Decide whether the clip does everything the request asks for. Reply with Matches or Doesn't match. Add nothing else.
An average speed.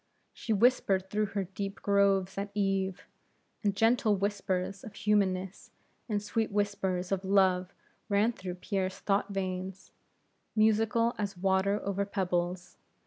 Doesn't match